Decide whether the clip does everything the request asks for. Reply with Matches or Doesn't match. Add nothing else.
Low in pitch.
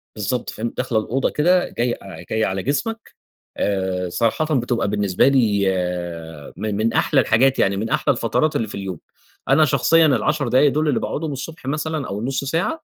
Matches